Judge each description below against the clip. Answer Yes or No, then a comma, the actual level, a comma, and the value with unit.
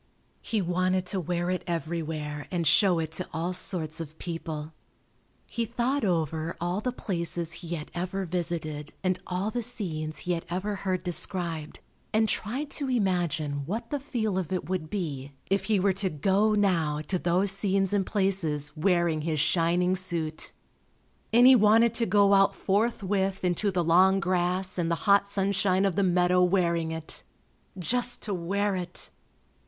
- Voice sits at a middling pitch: Yes, medium, 180 Hz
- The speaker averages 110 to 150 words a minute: No, average, 170 wpm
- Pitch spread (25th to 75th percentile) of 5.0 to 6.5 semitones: No, average, 3.1 semitones